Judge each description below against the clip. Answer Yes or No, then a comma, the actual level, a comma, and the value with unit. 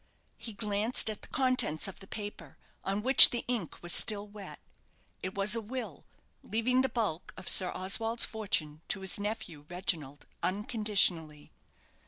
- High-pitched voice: Yes, high, 205 Hz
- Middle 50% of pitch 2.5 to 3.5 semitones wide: No, average, 3.9 semitones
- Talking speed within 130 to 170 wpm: Yes, average, 155 wpm